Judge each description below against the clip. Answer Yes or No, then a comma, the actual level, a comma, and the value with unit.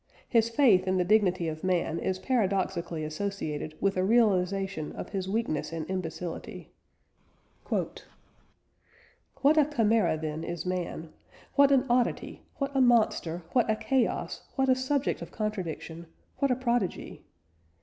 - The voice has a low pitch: No, high, 195 Hz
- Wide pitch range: Yes, wide, 5.9 semitones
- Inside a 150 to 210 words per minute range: No, average, 140 wpm